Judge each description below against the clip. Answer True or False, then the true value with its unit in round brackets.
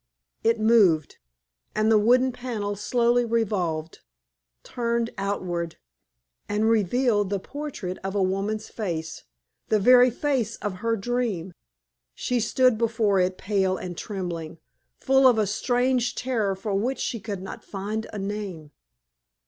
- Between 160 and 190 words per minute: False (135 wpm)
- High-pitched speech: True (215 Hz)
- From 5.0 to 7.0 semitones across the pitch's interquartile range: False (3.7 semitones)